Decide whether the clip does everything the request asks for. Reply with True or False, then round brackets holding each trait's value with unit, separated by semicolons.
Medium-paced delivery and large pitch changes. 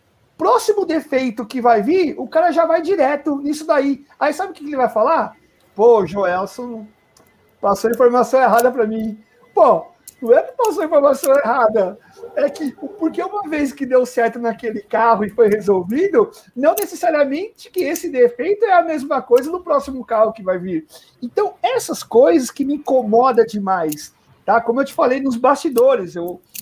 True (170 wpm; 6.6 semitones)